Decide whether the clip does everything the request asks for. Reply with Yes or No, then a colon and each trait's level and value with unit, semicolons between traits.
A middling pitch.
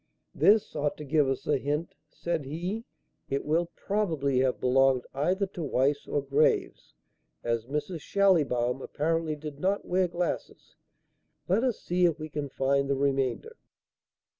Yes: medium, 150 Hz